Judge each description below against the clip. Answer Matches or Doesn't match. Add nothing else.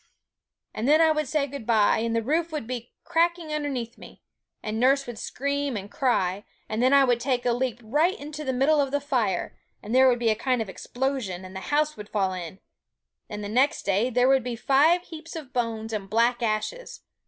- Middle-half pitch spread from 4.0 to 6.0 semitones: Matches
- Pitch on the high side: Matches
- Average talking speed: Doesn't match